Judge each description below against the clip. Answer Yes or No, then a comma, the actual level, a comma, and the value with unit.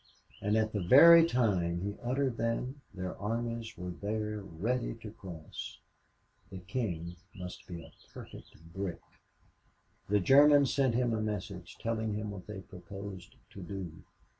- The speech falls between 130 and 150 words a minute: Yes, average, 145 wpm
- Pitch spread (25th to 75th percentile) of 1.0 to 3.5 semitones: No, average, 4.1 semitones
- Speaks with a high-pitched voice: No, low, 105 Hz